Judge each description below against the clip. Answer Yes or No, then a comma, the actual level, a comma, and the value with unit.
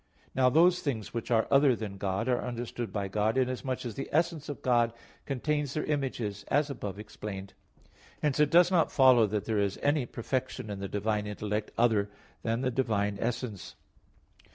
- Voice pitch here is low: Yes, low, 120 Hz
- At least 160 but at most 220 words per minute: Yes, average, 175 wpm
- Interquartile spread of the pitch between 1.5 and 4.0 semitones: No, average, 4.7 semitones